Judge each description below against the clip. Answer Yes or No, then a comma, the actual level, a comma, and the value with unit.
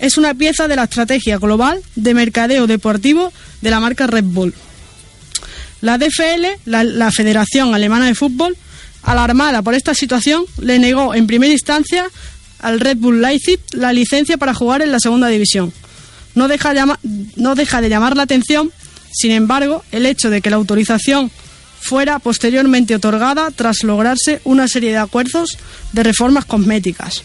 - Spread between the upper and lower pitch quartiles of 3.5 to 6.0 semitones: Yes, average, 3.9 semitones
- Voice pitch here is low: No, very high, 250 Hz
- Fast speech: No, average, 160 wpm